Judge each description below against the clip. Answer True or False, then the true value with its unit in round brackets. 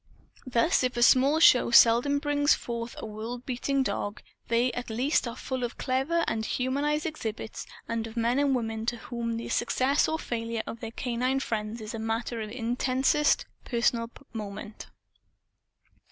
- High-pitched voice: True (240 Hz)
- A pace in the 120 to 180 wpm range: True (160 wpm)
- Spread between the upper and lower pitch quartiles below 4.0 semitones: True (2.6 semitones)